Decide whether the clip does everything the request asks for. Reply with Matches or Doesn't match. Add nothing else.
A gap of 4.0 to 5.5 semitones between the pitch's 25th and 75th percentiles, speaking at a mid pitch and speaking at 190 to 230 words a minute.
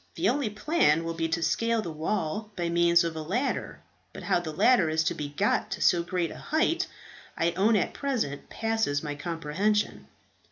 Matches